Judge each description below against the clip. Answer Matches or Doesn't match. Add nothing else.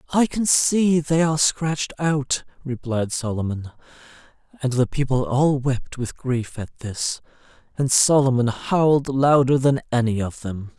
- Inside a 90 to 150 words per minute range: Matches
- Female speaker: Doesn't match